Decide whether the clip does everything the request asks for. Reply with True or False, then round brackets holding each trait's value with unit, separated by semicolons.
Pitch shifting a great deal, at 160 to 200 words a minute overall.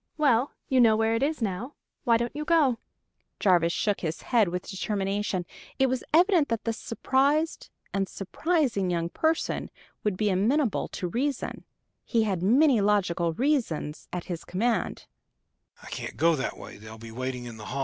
False (6.2 semitones; 135 wpm)